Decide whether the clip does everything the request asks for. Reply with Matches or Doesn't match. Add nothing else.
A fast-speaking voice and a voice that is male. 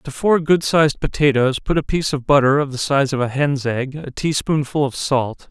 Matches